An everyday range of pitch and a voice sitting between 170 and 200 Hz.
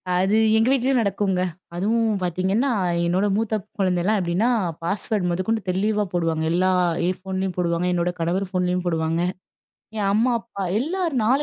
Yes: average, 3.6 semitones; high, 190 Hz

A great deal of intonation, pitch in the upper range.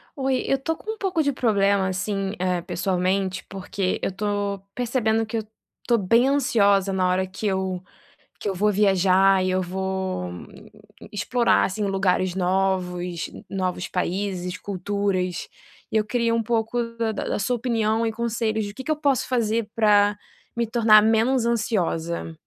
No: average, 3.6 semitones; high, 205 Hz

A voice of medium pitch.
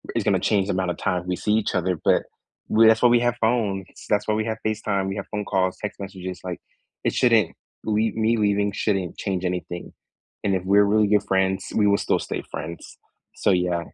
No: low, 100 Hz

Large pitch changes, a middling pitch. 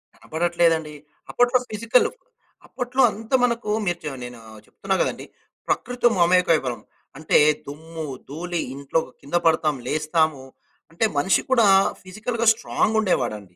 Yes: wide, 6.4 semitones; medium, 170 Hz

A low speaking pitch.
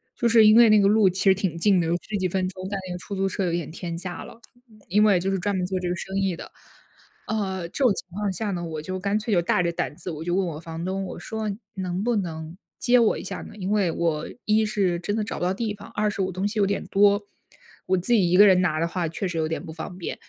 No: high, 190 Hz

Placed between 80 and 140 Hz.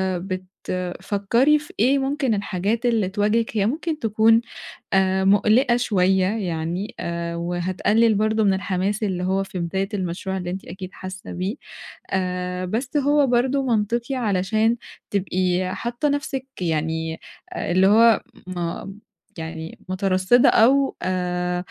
No: high, 195 Hz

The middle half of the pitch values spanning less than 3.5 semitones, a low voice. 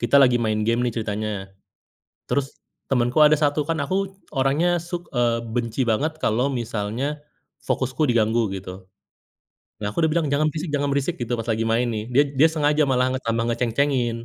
No: average, 3.9 semitones; low, 125 Hz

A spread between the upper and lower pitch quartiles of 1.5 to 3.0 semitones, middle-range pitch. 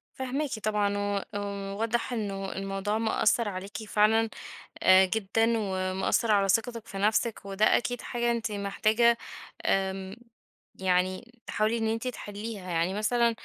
No: average, 2.7 semitones; high, 210 Hz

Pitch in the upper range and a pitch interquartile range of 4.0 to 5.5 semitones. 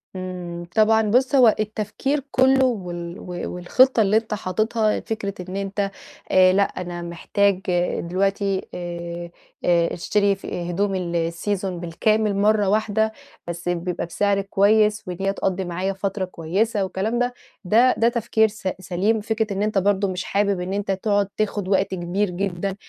No: high, 195 Hz; average, 3.0 semitones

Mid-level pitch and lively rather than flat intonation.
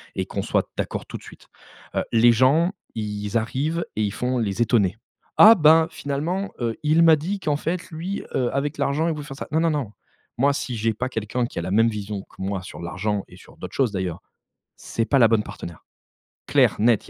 No: low, 120 Hz; wide, 6.4 semitones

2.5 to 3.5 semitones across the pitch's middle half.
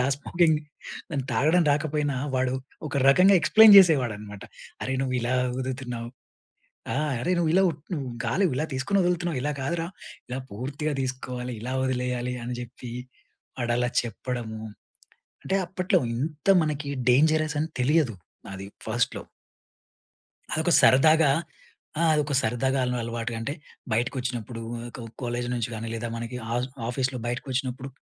No: average, 4.1 semitones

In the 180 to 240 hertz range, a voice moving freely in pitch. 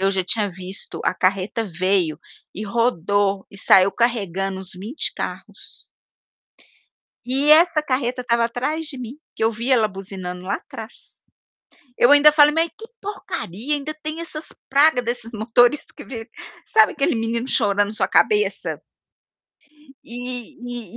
Yes: high, 235 Hz; wide, 5.9 semitones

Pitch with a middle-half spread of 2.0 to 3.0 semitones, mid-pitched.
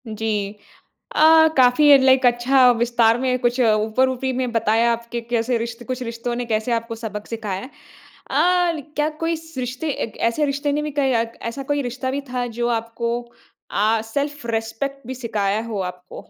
No: average, 2.7 semitones; high, 240 Hz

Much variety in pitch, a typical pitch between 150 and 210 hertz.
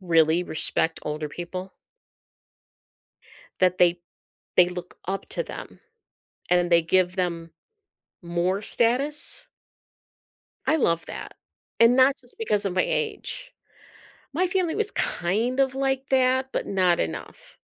Yes: wide, 7.2 semitones; high, 190 Hz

